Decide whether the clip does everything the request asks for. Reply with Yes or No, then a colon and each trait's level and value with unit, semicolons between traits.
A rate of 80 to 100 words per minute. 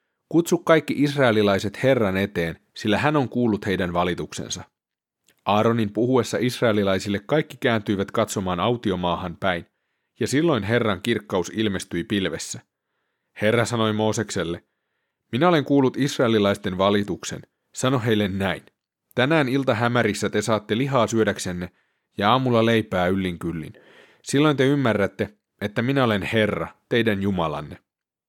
No: average, 120 wpm